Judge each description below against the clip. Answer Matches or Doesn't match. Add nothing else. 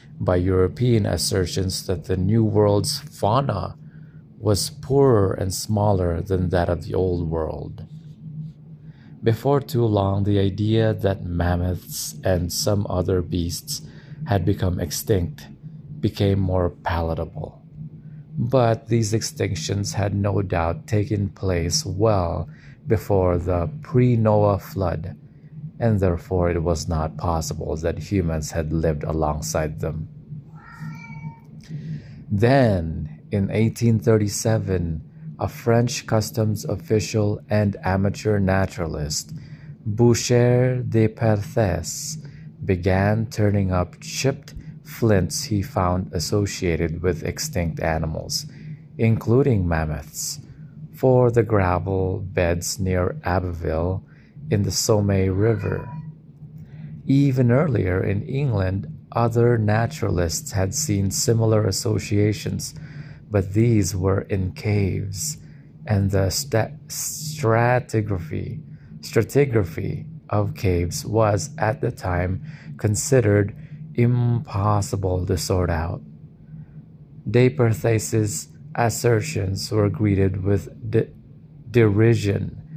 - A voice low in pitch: Matches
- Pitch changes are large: Matches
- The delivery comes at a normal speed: Doesn't match